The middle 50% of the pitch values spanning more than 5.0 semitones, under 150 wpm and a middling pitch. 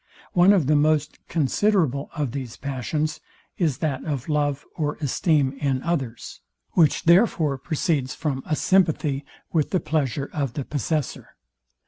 No: average, 2.9 semitones; average, 140 wpm; medium, 150 Hz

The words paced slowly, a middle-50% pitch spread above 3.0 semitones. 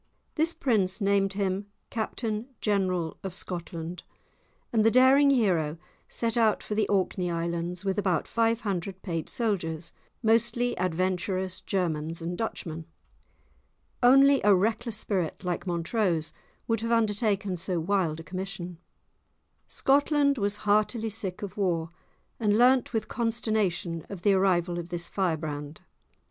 Yes: slow, 130 wpm; average, 4.3 semitones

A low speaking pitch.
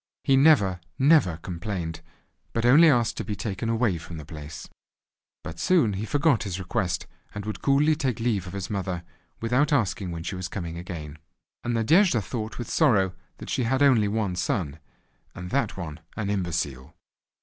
Yes: low, 100 Hz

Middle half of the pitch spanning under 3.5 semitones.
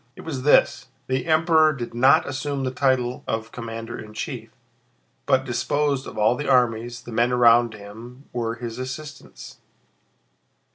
Yes: average, 2.9 semitones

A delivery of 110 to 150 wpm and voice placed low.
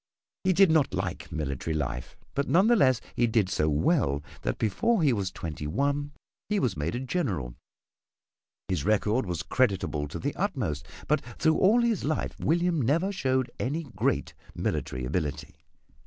No: average, 165 wpm; low, 125 Hz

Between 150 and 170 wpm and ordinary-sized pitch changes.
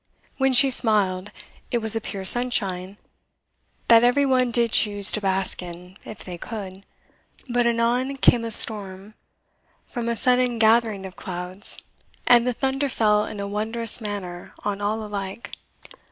Yes: average, 155 wpm; average, 3.5 semitones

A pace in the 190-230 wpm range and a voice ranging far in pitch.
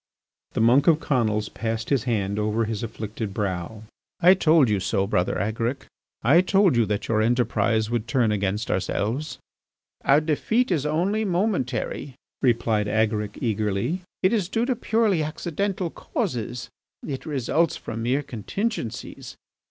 No: average, 145 wpm; wide, 7.1 semitones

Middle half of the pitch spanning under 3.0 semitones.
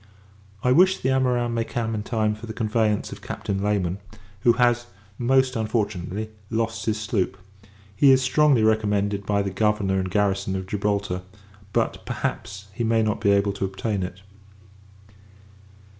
Yes: narrow, 2.6 semitones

